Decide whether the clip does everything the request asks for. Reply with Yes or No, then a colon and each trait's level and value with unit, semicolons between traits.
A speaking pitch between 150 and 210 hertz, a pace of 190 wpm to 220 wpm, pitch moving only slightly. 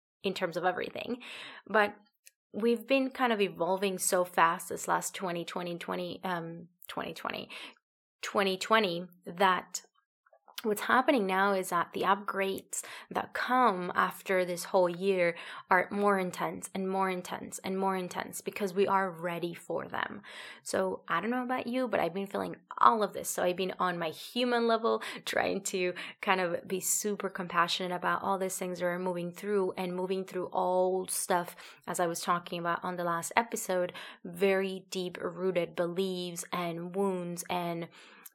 No: medium, 185 Hz; average, 165 wpm; narrow, 1.9 semitones